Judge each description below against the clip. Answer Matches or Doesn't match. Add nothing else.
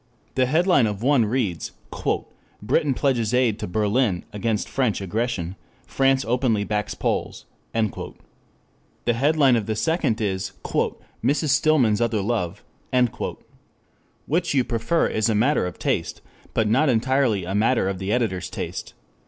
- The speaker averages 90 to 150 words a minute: Matches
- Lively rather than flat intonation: Doesn't match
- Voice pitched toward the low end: Matches